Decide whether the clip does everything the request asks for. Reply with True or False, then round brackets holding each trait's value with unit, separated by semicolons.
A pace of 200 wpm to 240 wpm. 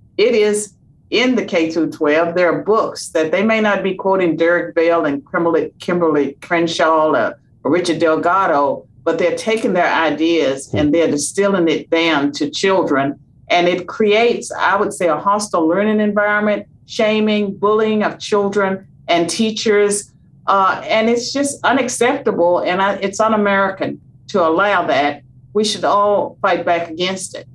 False (155 wpm)